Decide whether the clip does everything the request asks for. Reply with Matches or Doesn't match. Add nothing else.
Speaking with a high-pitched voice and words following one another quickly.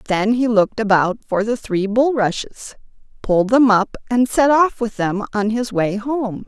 Doesn't match